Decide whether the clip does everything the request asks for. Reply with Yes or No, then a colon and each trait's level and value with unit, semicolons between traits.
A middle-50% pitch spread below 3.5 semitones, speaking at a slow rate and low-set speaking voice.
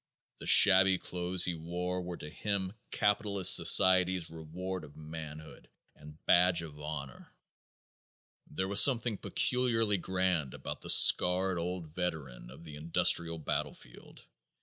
Yes: average, 3.1 semitones; slow, 125 wpm; very low, 90 Hz